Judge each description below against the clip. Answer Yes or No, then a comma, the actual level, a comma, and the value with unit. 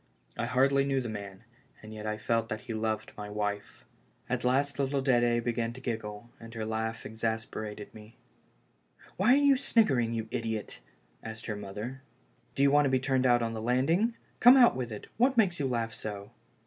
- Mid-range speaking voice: No, low, 115 Hz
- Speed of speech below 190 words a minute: No, average, 200 wpm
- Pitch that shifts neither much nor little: Yes, average, 3.7 semitones